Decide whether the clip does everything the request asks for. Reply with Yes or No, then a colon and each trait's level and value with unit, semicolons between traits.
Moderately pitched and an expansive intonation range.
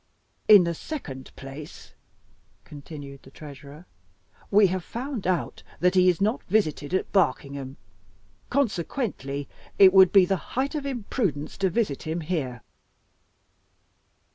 Yes: medium, 180 Hz; wide, 6.3 semitones